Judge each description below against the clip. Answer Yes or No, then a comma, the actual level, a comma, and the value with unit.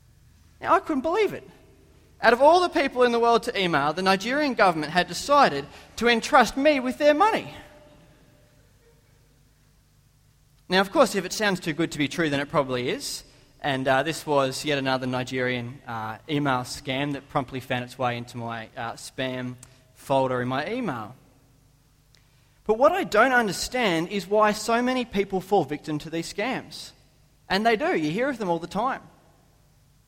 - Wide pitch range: Yes, wide, 8.4 semitones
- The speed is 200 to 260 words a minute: No, average, 180 wpm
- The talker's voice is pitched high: No, medium, 150 Hz